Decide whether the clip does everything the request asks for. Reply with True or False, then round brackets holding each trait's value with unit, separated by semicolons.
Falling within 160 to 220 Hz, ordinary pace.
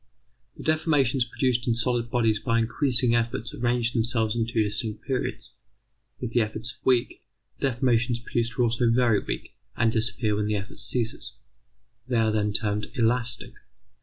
False (115 Hz; 165 wpm)